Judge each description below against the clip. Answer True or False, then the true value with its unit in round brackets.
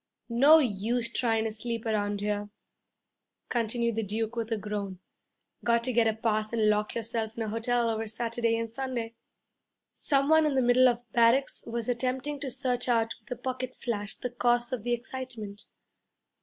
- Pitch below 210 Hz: False (235 Hz)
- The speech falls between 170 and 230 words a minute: True (180 wpm)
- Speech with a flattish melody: True (2.1 semitones)